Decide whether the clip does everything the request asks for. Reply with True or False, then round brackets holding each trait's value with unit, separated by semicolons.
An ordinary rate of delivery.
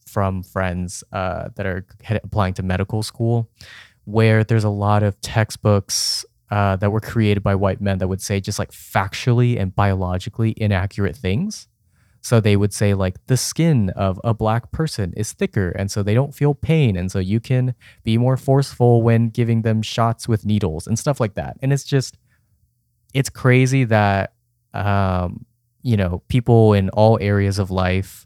True (180 wpm)